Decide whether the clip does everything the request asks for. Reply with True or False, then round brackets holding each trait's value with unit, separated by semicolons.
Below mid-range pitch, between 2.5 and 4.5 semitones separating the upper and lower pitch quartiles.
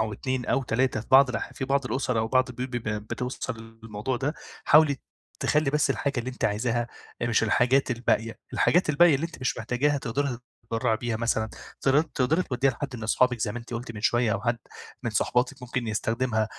True (125 Hz; 3.1 semitones)